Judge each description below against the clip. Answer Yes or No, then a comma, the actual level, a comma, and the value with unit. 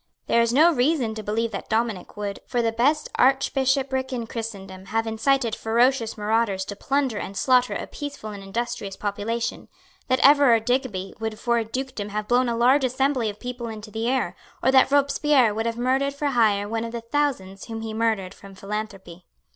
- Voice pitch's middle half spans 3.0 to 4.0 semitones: Yes, average, 3.7 semitones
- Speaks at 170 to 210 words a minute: Yes, average, 190 wpm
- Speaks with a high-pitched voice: Yes, high, 230 Hz